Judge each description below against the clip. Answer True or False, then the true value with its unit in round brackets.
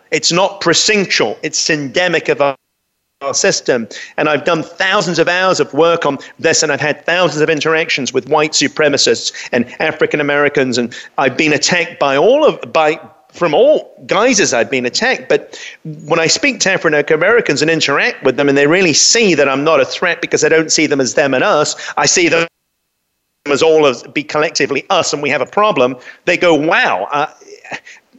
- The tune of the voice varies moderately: True (3.1 semitones)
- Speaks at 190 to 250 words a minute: True (195 wpm)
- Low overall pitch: False (160 Hz)